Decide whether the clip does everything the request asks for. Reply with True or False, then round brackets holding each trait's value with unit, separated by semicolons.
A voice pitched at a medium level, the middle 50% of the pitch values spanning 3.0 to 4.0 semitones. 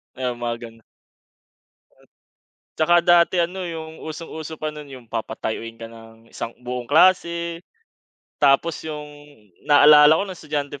False (150 Hz; 5.3 semitones)